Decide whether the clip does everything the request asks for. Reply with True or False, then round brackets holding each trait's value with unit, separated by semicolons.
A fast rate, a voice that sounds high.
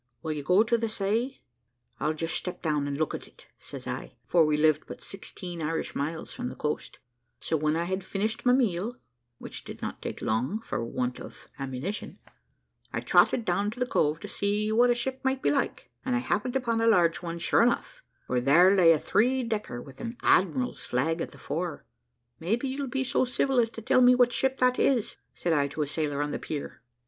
True (220 wpm; 195 Hz)